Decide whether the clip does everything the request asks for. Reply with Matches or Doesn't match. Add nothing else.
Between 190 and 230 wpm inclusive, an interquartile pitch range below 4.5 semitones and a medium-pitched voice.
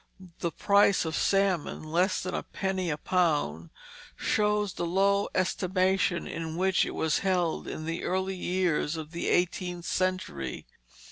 Doesn't match